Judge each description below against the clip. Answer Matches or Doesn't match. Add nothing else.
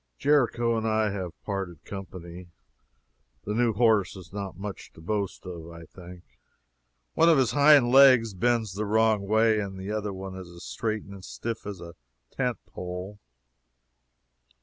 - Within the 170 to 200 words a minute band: Doesn't match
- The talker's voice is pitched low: Matches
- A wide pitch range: Doesn't match